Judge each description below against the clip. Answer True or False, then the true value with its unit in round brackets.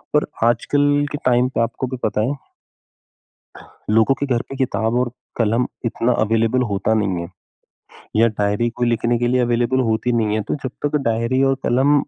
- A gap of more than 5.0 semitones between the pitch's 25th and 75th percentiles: False (2.5 semitones)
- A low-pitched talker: True (120 Hz)